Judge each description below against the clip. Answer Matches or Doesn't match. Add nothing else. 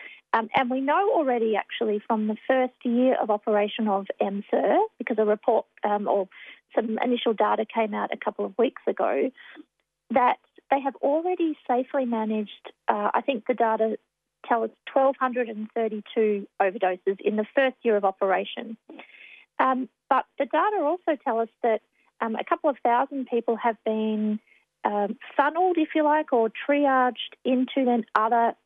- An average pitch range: Matches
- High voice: Matches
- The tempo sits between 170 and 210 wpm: Doesn't match